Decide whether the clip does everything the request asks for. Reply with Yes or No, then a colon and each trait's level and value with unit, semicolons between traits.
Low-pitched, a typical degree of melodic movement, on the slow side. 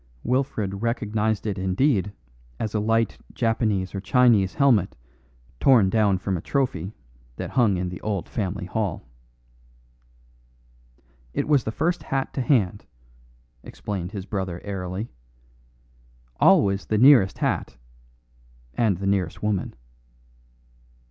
Yes: low, 105 Hz; average, 3.3 semitones; slow, 120 wpm